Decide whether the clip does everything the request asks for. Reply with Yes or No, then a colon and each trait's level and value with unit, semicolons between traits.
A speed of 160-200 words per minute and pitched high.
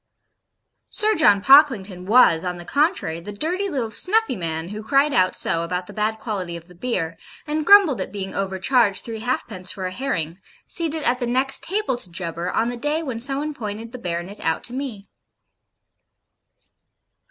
Yes: average, 180 wpm; high, 220 Hz